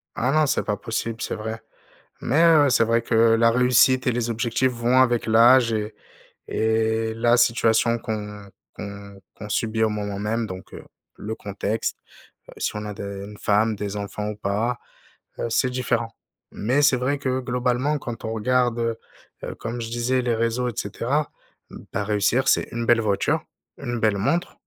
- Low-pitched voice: Yes, low, 115 Hz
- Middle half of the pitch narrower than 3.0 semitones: Yes, narrow, 2.6 semitones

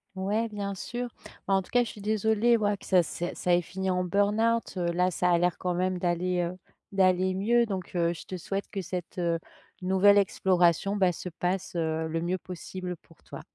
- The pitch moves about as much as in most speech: No, narrow, 2.3 semitones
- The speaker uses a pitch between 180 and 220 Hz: Yes, medium, 185 Hz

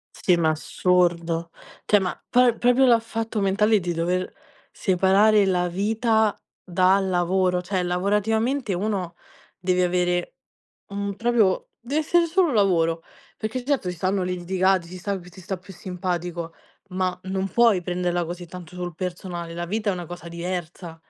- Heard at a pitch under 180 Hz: No, medium, 185 Hz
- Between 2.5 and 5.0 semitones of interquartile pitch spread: Yes, average, 2.8 semitones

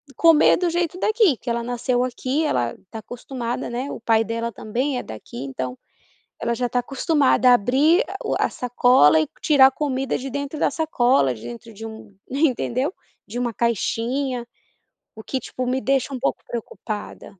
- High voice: Yes, high, 245 Hz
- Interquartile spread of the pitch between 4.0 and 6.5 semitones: No, average, 3.3 semitones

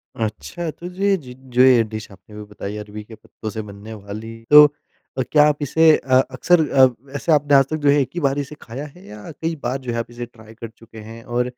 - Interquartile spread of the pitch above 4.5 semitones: Yes, average, 4.9 semitones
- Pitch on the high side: No, low, 125 Hz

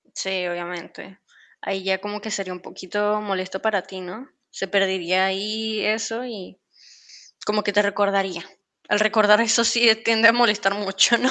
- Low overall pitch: No, high, 205 Hz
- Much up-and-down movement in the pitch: No, narrow, 2.4 semitones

